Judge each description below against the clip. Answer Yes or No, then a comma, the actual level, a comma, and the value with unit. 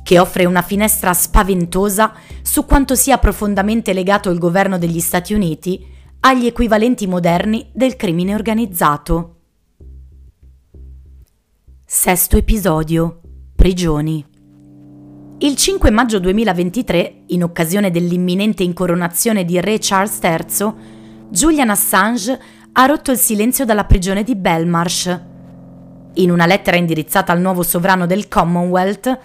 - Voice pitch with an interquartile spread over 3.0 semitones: Yes, average, 4.3 semitones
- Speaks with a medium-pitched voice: Yes, medium, 180 Hz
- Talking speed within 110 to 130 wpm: Yes, slow, 115 wpm